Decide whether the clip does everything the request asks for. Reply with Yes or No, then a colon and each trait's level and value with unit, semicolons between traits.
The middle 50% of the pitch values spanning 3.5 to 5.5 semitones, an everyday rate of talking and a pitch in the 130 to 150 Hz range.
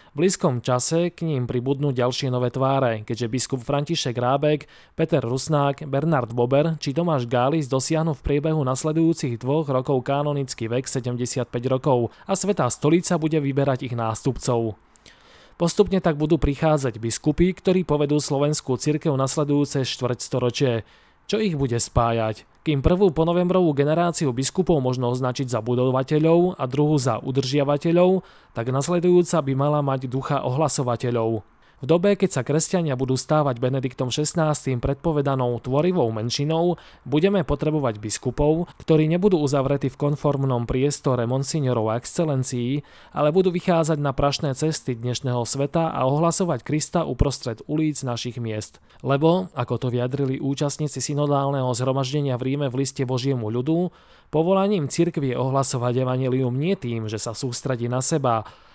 Yes: average, 3.8 semitones; average, 140 wpm; medium, 140 Hz